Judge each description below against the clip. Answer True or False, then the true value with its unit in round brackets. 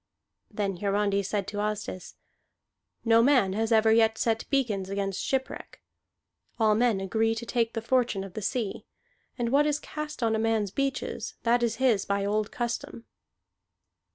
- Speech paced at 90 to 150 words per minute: False (160 wpm)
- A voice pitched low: False (225 Hz)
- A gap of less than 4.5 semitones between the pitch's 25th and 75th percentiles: True (2.9 semitones)